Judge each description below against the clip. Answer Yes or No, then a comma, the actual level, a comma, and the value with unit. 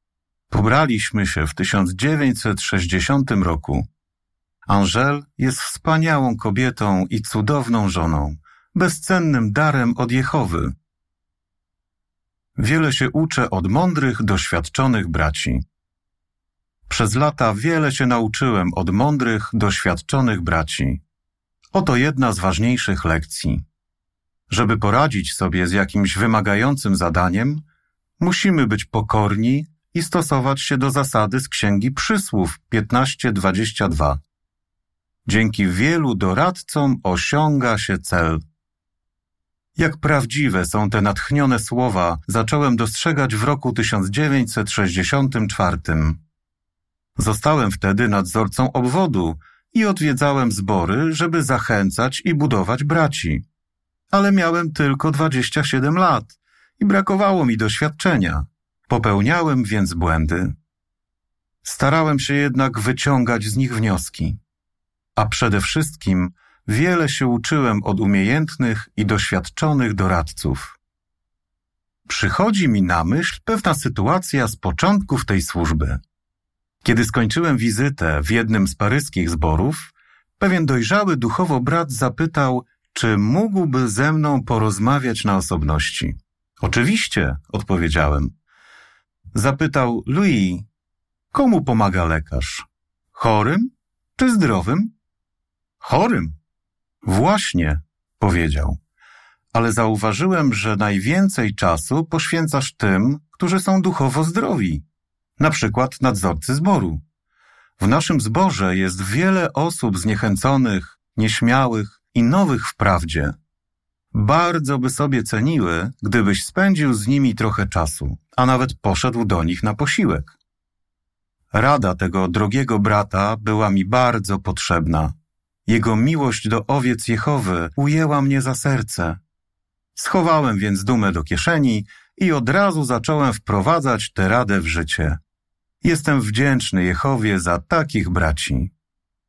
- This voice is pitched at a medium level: No, low, 110 Hz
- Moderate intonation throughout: No, wide, 7.6 semitones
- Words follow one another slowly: Yes, slow, 105 wpm